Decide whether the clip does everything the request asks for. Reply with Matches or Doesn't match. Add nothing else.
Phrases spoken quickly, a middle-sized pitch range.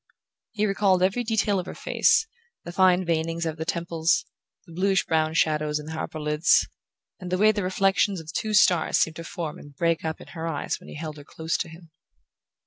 Matches